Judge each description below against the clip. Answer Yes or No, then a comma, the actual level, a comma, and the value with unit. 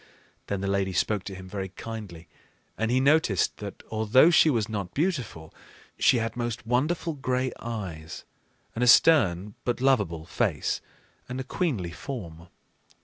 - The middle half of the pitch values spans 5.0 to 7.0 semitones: Yes, average, 5.3 semitones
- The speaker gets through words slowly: No, average, 150 wpm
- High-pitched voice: No, low, 110 Hz